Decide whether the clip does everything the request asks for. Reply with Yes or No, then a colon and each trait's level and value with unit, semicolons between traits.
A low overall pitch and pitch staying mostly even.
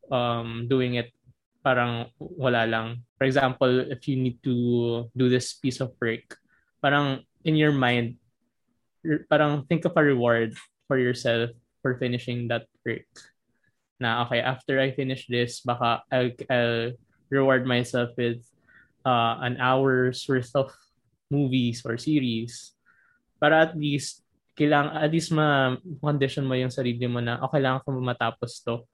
Yes: low, 125 Hz; narrow, 2.3 semitones